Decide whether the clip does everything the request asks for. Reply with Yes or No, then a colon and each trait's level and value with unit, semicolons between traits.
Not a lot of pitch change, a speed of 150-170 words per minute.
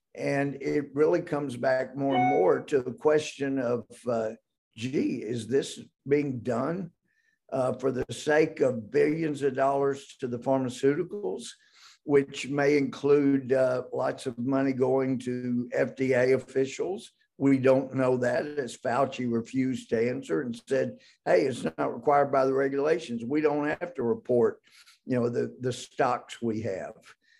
Yes: narrow, 2.2 semitones; average, 155 wpm